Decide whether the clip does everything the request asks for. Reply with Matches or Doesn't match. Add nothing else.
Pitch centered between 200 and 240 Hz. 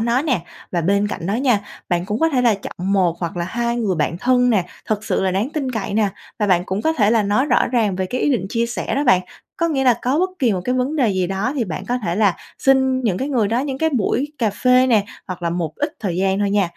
Matches